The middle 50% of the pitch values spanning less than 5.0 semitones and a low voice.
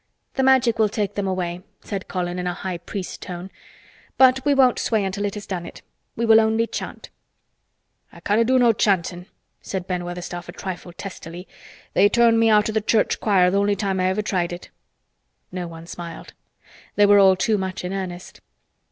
No: average, 3.4 semitones; high, 195 Hz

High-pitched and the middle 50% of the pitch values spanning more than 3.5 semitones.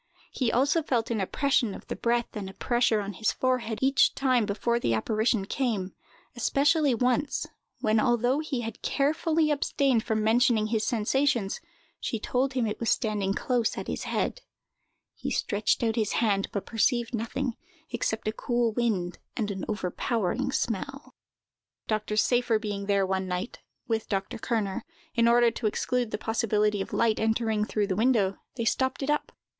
No: high, 230 Hz; average, 3.0 semitones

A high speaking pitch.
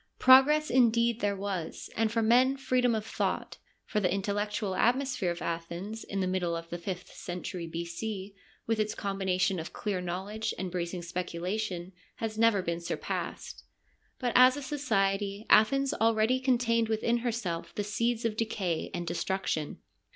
Yes: high, 205 Hz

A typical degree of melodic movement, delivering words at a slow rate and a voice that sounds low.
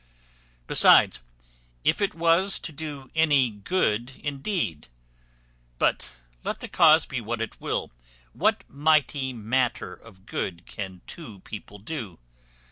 No: wide, 7.1 semitones; slow, 125 wpm; low, 130 Hz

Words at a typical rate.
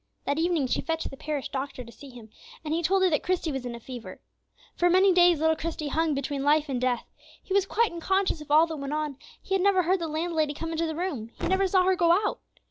No: fast, 255 wpm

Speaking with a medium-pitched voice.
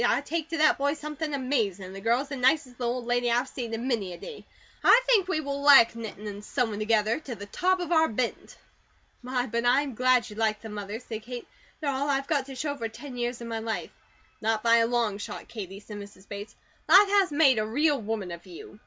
No: high, 245 Hz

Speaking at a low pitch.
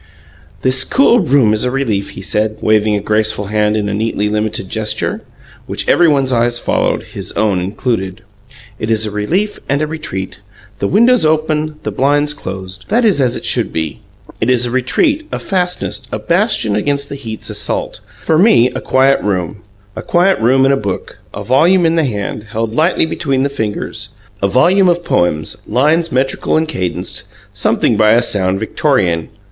Yes: low, 120 Hz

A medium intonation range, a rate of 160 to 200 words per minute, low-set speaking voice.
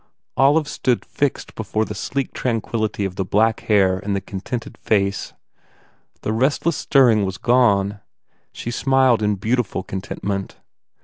No: average, 4.2 semitones; average, 140 wpm; low, 110 Hz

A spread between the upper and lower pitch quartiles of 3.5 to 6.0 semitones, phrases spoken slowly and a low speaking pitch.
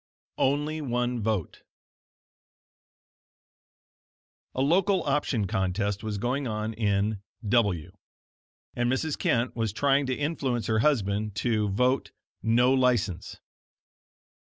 Yes: average, 4.3 semitones; slow, 105 wpm; low, 120 Hz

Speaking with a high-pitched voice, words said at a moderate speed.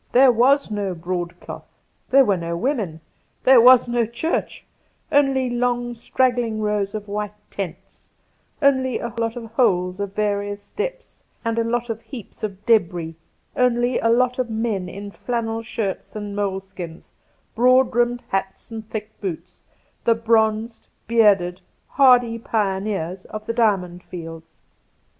Yes: high, 220 Hz; average, 145 wpm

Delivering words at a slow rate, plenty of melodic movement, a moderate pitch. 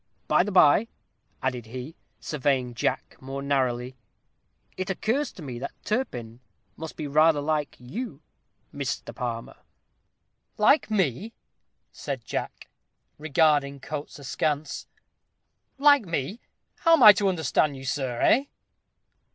Yes: slow, 120 wpm; wide, 6.5 semitones; medium, 150 Hz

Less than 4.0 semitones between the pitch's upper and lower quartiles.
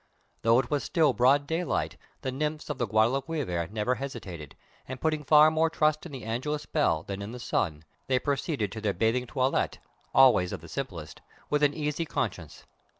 No: wide, 5.6 semitones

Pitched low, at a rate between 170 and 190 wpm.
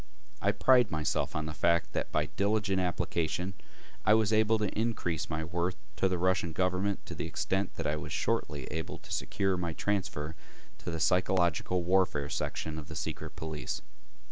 Yes: very low, 90 Hz; average, 175 wpm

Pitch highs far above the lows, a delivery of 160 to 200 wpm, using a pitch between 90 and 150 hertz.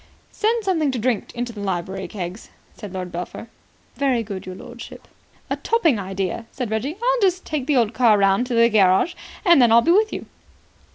No: wide, 7.3 semitones; average, 195 wpm; high, 235 Hz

